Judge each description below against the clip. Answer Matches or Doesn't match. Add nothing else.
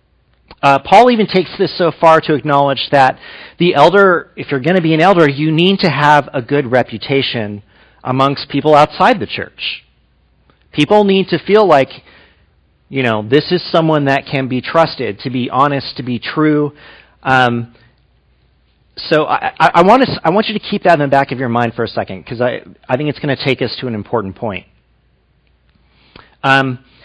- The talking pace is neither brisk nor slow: Matches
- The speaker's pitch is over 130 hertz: Matches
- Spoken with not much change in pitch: Doesn't match